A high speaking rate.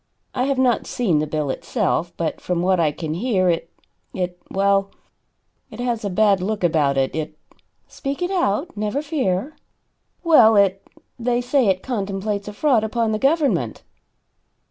No: average, 165 wpm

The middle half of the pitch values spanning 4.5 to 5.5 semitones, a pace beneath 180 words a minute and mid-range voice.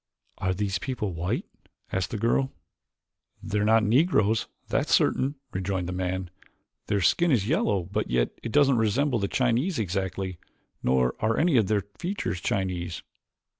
No: average, 4.8 semitones; average, 150 wpm; low, 105 Hz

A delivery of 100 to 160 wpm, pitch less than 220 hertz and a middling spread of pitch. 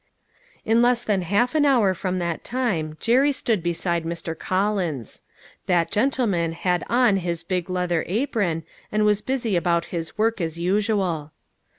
Yes: average, 155 wpm; medium, 185 Hz; average, 4.9 semitones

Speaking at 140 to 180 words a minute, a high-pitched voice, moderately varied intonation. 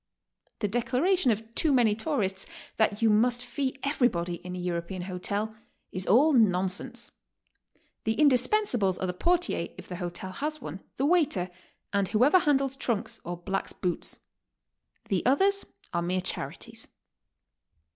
No: average, 145 wpm; high, 220 Hz; wide, 6.7 semitones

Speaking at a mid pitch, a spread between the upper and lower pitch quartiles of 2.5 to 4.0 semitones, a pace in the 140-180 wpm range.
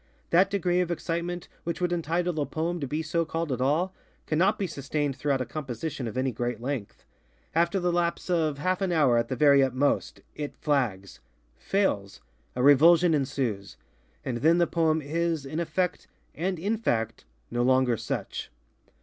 No: medium, 155 Hz; average, 4.7 semitones; average, 165 wpm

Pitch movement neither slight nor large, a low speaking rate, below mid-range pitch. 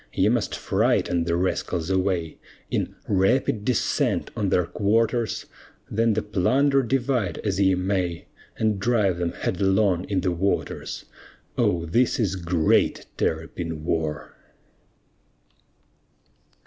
Yes: average, 3.9 semitones; slow, 115 wpm; very low, 95 Hz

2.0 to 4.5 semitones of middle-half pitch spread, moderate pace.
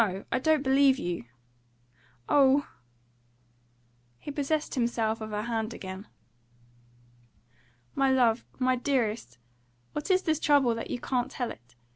No: average, 4.0 semitones; slow, 125 wpm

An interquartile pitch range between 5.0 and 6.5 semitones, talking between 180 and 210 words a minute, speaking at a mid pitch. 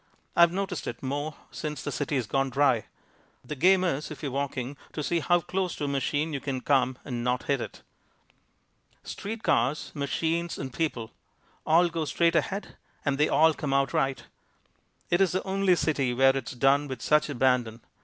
No: average, 3.9 semitones; average, 185 wpm; medium, 145 Hz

